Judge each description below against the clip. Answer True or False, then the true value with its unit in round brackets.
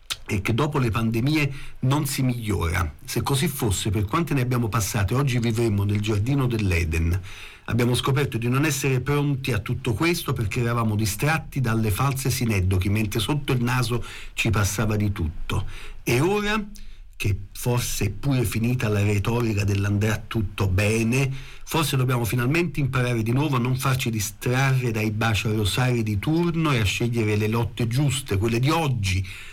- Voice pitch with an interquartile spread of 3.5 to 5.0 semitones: True (4.3 semitones)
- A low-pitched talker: True (120 Hz)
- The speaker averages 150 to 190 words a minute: True (165 wpm)